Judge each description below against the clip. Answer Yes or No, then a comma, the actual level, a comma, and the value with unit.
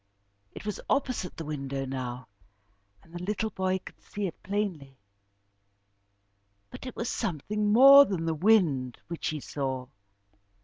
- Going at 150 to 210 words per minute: No, average, 140 wpm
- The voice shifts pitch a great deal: Yes, wide, 7.4 semitones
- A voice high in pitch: No, medium, 175 Hz